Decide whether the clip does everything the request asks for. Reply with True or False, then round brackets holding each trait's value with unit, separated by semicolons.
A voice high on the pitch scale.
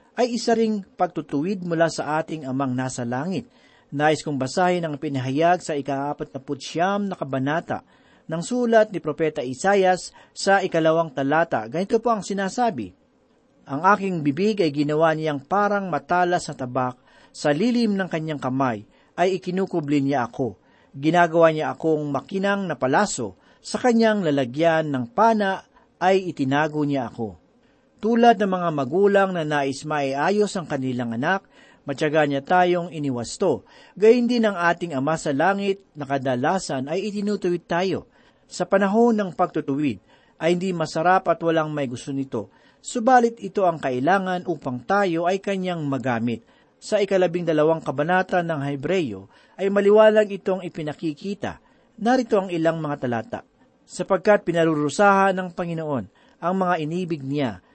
False (170 Hz)